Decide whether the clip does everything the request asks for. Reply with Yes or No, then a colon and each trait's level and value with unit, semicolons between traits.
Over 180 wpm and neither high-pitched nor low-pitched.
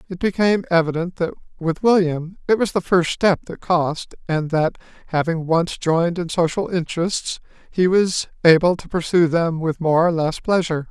No: average, 175 wpm; medium, 170 Hz